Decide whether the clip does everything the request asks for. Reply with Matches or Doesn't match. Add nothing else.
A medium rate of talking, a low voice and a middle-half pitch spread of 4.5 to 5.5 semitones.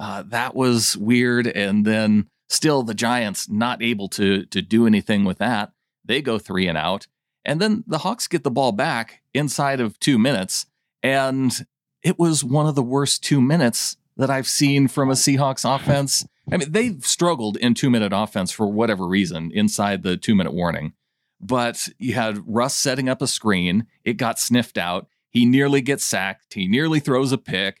Matches